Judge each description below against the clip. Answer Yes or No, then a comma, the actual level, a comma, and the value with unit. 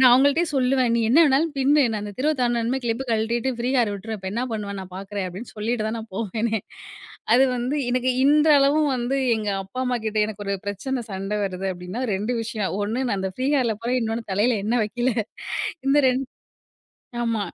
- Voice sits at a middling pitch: No, high, 235 Hz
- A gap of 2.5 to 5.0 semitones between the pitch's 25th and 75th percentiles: Yes, average, 3.6 semitones